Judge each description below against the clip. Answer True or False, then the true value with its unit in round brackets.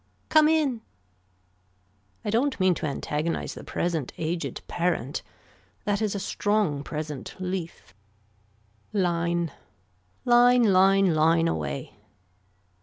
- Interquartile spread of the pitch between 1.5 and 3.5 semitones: False (4.8 semitones)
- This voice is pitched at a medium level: True (175 Hz)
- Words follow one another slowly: True (105 wpm)